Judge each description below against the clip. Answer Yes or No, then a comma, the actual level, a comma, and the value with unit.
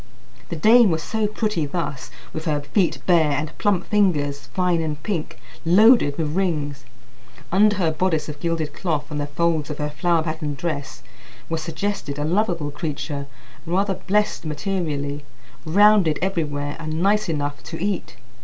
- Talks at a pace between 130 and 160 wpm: Yes, average, 155 wpm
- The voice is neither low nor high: Yes, medium, 160 Hz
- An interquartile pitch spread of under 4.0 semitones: No, average, 4.3 semitones